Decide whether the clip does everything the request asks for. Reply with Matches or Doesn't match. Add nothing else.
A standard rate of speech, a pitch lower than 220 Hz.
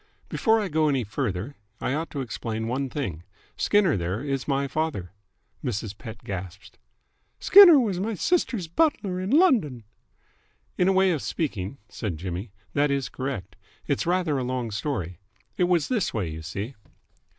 Matches